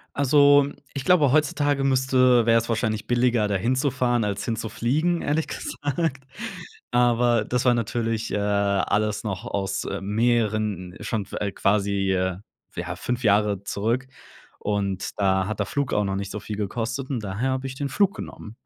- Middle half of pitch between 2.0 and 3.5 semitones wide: No, average, 4.3 semitones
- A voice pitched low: Yes, low, 115 Hz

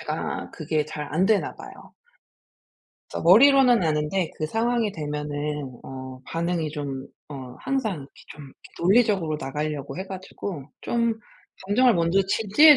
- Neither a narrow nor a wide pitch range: No, wide, 6.0 semitones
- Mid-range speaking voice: Yes, medium, 165 Hz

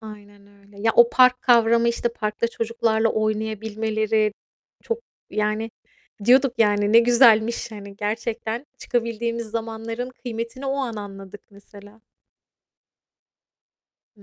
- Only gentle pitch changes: Yes, narrow, 1.8 semitones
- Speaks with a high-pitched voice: Yes, high, 225 Hz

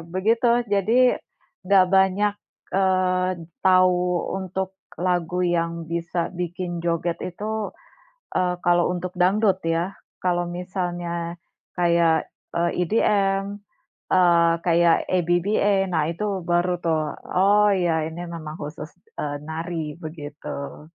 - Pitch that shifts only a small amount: Yes, narrow, 2.1 semitones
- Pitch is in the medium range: Yes, medium, 180 Hz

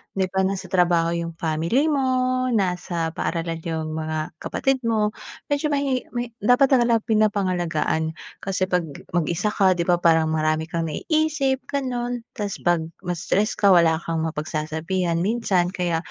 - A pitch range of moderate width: No, wide, 6.3 semitones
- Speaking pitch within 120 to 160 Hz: No, medium, 185 Hz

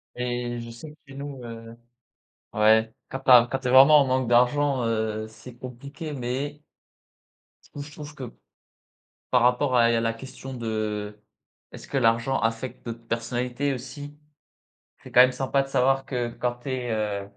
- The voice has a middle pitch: No, low, 125 Hz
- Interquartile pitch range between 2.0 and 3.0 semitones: Yes, narrow, 2.6 semitones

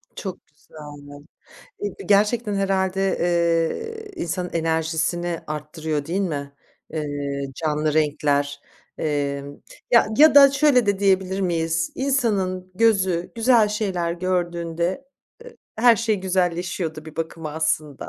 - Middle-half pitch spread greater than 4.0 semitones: Yes, average, 4.4 semitones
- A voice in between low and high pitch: Yes, medium, 175 Hz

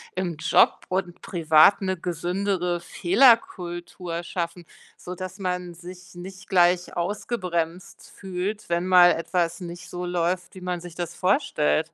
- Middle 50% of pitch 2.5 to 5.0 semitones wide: No, narrow, 1.4 semitones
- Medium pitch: Yes, medium, 180 Hz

